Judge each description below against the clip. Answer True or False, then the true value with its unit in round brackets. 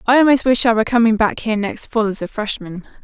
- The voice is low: False (225 Hz)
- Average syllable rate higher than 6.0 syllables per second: True (6.6 syllables/s)